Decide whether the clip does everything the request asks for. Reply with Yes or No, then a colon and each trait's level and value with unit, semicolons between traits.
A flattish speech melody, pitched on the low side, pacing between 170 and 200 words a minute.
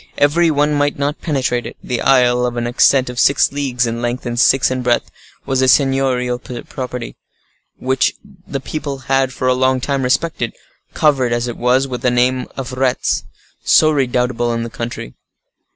Yes: narrow, 1.9 semitones; low, 130 Hz; average, 180 wpm